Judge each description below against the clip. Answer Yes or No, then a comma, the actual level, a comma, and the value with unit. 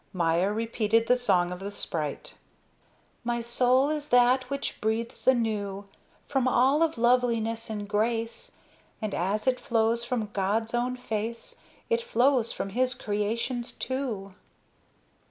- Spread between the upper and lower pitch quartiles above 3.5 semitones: No, average, 3.1 semitones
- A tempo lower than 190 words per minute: Yes, slow, 135 wpm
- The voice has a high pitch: Yes, high, 230 Hz